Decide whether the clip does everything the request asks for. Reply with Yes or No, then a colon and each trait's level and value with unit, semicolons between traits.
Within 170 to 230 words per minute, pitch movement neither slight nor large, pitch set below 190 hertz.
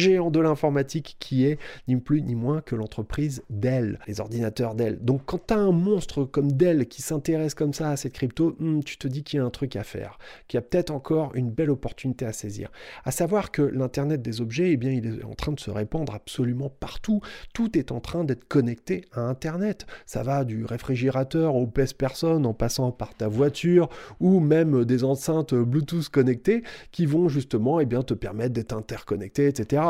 Yes: average, 210 wpm; average, 4.8 semitones; medium, 140 Hz